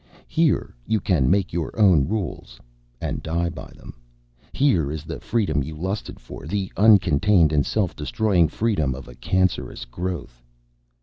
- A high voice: No, very low, 85 Hz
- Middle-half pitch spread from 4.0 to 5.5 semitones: Yes, average, 5.1 semitones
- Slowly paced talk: No, average, 150 wpm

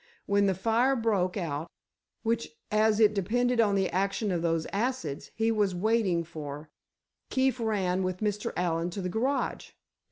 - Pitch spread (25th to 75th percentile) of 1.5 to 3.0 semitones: No, average, 4.1 semitones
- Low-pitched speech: No, high, 200 Hz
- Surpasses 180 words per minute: No, average, 155 wpm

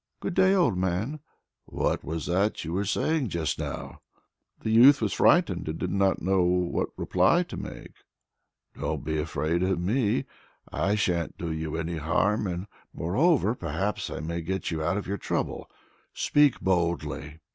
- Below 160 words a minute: No, average, 165 wpm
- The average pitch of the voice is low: Yes, very low, 95 Hz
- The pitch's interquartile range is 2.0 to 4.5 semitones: Yes, average, 4.1 semitones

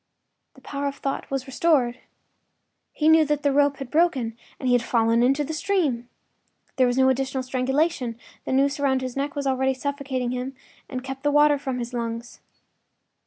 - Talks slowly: No, average, 185 wpm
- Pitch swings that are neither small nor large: No, narrow, 2.3 semitones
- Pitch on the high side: Yes, very high, 265 Hz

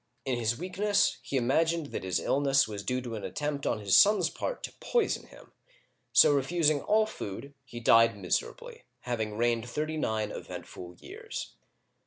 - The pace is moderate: Yes, average, 165 wpm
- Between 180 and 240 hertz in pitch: No, low, 130 Hz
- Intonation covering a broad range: Yes, wide, 5.7 semitones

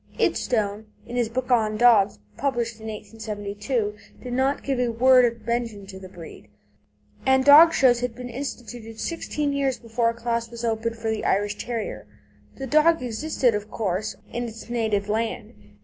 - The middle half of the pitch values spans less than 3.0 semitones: Yes, narrow, 2.6 semitones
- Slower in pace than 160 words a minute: No, average, 170 wpm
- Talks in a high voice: Yes, high, 230 Hz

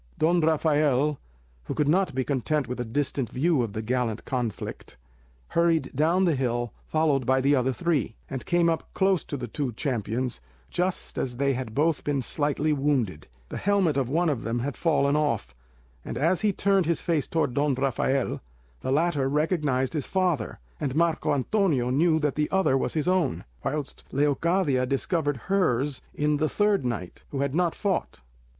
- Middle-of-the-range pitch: Yes, medium, 145 Hz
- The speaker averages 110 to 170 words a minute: No, average, 180 wpm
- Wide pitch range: No, average, 4.3 semitones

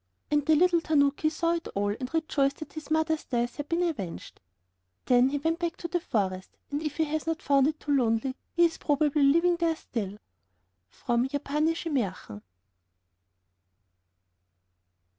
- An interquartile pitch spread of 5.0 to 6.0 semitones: No, average, 4.2 semitones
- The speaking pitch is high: Yes, very high, 295 Hz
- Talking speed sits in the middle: Yes, average, 160 wpm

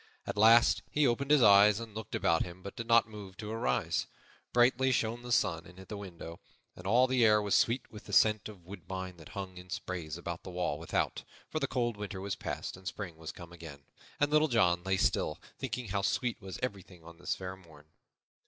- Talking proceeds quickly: Yes, fast, 220 wpm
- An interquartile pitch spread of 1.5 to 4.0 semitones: No, average, 4.7 semitones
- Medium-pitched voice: No, low, 100 Hz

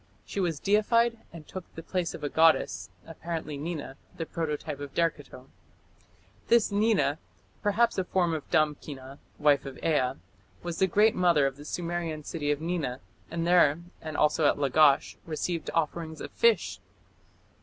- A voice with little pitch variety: No, average, 3.2 semitones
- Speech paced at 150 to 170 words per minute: Yes, average, 155 wpm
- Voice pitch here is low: No, medium, 160 Hz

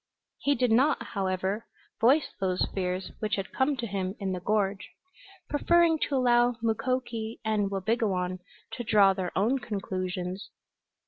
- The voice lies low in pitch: No, high, 215 Hz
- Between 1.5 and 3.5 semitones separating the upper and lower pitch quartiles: No, average, 4.3 semitones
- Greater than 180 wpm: No, average, 140 wpm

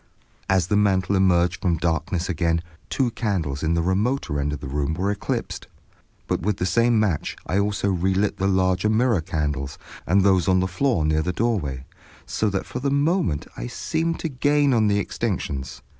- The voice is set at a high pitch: No, very low, 95 Hz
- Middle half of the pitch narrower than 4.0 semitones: No, average, 4.6 semitones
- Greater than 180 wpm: Yes, average, 190 wpm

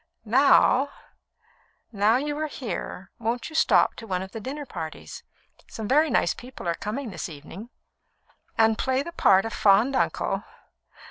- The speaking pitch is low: No, high, 225 Hz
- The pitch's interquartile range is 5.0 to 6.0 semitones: Yes, wide, 5.5 semitones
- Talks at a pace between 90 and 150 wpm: No, average, 160 wpm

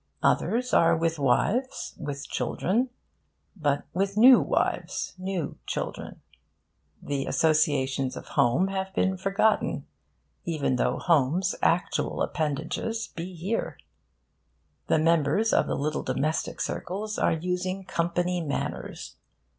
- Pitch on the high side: No, medium, 170 Hz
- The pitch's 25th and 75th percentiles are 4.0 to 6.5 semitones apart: Yes, average, 4.3 semitones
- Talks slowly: Yes, slow, 115 wpm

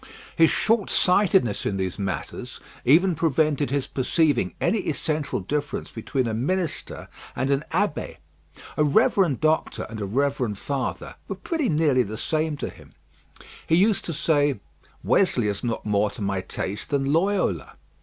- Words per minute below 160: Yes, average, 150 wpm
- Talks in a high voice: No, medium, 145 Hz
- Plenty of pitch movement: Yes, wide, 6.4 semitones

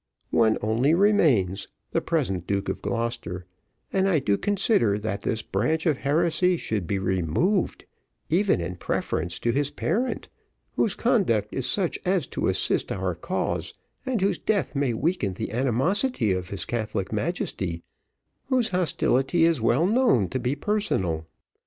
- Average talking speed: Yes, average, 150 wpm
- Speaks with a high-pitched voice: No, low, 130 Hz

